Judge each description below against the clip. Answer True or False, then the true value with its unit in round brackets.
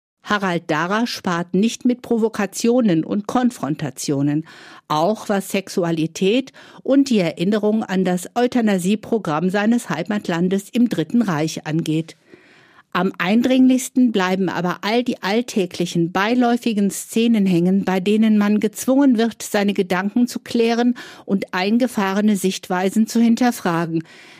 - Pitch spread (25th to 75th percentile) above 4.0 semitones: True (4.6 semitones)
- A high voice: True (205 Hz)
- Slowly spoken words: True (115 wpm)